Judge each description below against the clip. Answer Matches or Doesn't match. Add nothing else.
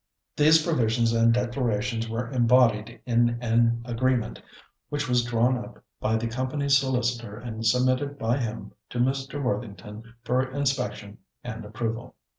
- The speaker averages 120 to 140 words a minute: Matches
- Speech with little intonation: Matches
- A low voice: Matches